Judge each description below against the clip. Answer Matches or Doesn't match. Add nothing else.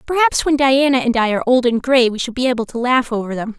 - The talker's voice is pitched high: Matches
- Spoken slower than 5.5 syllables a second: Doesn't match